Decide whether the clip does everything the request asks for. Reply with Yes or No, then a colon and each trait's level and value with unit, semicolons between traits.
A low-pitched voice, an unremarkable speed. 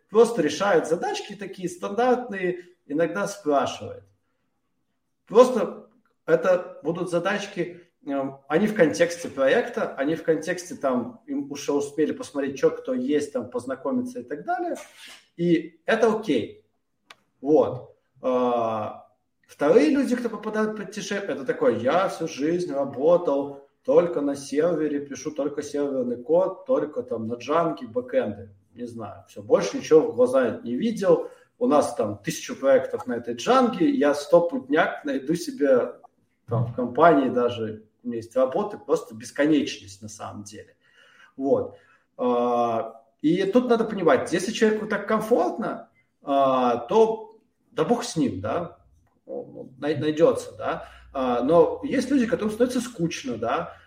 No: medium, 180 Hz; average, 130 wpm